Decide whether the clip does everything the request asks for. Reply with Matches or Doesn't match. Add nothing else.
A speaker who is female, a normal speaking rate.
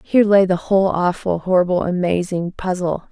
Matches